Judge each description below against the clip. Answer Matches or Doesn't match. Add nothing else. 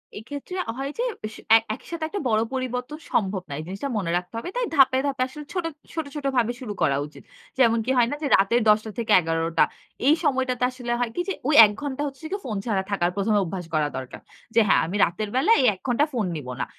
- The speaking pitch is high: Matches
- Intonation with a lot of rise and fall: Matches